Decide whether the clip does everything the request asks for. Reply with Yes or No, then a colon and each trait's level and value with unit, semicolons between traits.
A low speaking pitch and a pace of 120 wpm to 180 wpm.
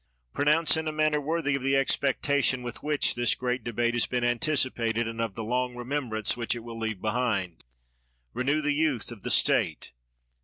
No: low, 125 Hz; average, 190 wpm